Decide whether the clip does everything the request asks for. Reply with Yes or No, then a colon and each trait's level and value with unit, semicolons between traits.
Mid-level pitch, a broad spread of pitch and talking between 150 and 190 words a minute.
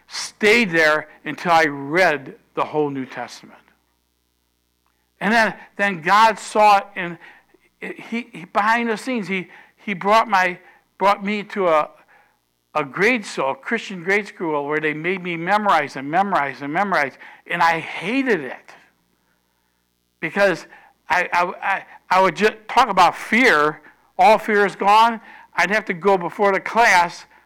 Yes: medium, 180 Hz; wide, 6.1 semitones; average, 155 wpm